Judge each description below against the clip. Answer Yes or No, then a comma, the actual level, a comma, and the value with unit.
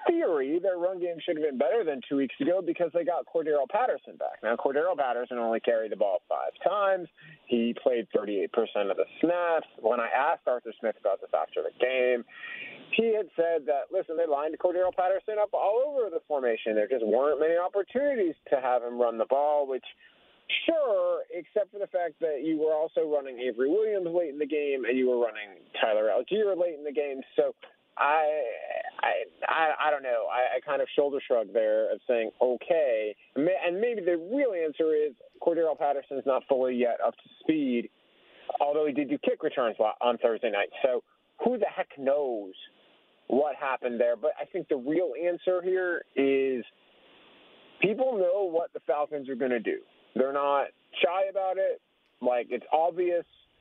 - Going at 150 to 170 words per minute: No, average, 190 wpm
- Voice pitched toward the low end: No, medium, 175 Hz